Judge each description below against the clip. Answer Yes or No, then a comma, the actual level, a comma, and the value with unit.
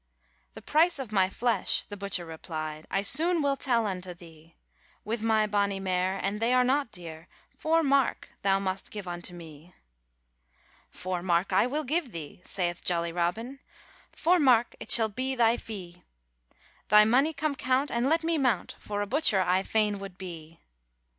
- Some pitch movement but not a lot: No, wide, 6.2 semitones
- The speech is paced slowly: No, average, 175 wpm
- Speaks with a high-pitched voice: Yes, high, 205 Hz